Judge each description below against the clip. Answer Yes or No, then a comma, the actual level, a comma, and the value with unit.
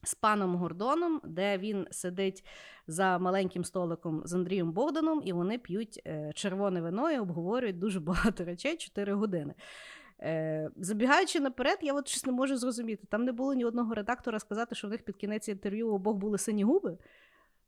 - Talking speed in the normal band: No, fast, 165 wpm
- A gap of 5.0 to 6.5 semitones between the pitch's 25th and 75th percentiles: Yes, wide, 5.5 semitones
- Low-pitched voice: No, high, 210 Hz